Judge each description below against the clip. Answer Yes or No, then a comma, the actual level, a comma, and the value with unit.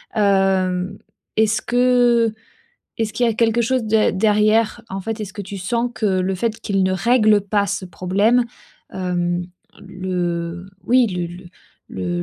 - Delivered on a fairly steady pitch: No, average, 3.4 semitones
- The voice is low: No, high, 205 Hz